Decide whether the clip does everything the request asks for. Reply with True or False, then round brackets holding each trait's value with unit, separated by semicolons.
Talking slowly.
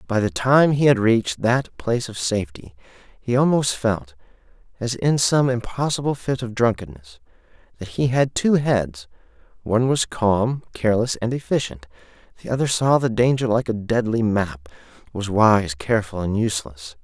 False (160 wpm)